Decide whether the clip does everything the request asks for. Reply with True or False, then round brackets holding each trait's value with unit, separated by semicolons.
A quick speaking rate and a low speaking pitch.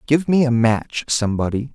False (170 wpm; 125 Hz)